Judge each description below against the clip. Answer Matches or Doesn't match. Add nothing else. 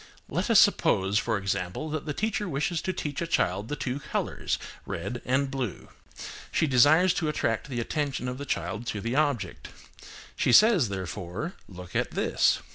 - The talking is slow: Doesn't match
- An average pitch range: Doesn't match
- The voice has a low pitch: Matches